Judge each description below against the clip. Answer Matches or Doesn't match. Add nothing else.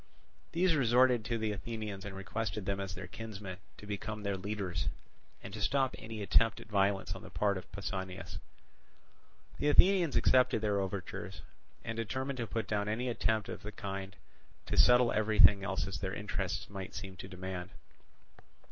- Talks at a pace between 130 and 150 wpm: Doesn't match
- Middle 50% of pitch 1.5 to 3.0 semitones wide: Matches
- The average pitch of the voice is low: Matches